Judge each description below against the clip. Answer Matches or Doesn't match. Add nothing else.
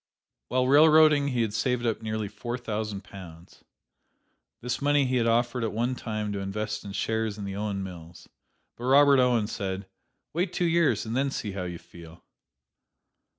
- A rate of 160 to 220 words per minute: Matches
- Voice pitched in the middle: Doesn't match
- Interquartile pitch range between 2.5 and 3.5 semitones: Doesn't match